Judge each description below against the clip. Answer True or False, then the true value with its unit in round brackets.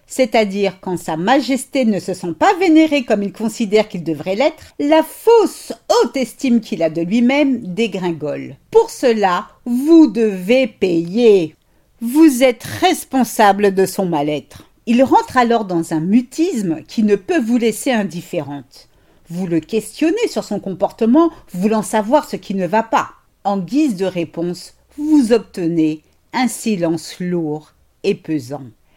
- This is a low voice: False (220 Hz)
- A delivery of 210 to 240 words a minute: False (150 wpm)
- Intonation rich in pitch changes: True (6.6 semitones)